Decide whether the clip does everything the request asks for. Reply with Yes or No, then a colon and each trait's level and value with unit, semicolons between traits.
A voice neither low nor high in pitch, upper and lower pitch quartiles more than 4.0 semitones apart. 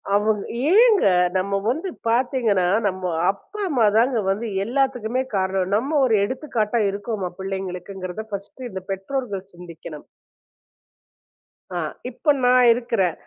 No: high, 210 Hz; average, 4.7 semitones